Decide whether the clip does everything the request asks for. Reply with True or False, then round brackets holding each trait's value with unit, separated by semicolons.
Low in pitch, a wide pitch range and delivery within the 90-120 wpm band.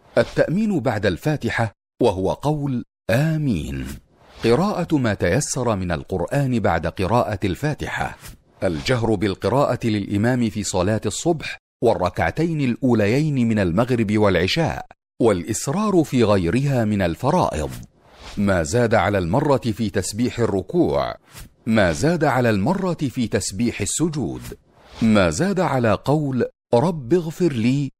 True (115 Hz; 5.8 semitones; 110 wpm)